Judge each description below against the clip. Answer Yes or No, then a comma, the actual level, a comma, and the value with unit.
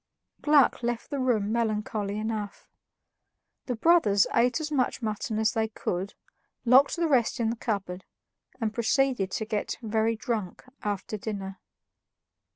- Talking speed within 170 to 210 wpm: No, average, 140 wpm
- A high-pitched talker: Yes, high, 220 Hz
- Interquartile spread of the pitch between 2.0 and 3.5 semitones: Yes, average, 3.1 semitones